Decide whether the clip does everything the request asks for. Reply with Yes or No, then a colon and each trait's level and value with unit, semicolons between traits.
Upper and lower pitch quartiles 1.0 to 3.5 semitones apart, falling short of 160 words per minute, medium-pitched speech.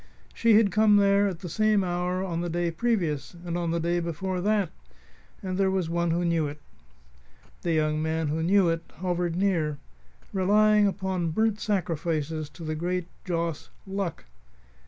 No: average, 3.0 semitones; average, 170 wpm; medium, 175 Hz